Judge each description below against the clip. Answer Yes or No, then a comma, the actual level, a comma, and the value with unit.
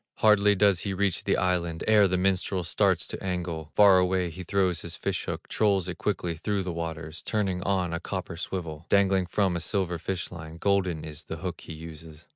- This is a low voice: Yes, very low, 90 Hz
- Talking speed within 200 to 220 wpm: Yes, fast, 205 wpm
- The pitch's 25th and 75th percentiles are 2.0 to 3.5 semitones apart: Yes, average, 2.7 semitones